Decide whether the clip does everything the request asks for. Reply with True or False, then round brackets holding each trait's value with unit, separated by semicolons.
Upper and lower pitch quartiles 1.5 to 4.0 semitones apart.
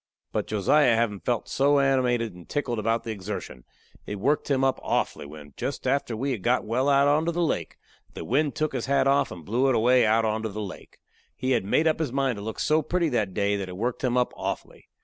False (4.5 semitones)